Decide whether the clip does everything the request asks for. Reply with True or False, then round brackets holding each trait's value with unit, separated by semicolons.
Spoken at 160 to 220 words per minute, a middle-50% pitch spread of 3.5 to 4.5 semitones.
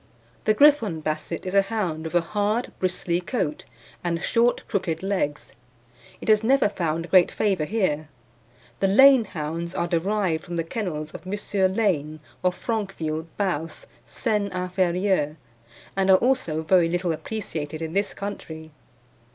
False (145 wpm; 4.2 semitones)